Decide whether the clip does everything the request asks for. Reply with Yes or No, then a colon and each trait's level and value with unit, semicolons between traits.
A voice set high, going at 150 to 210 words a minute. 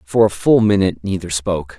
No: very low, 95 Hz; average, 200 wpm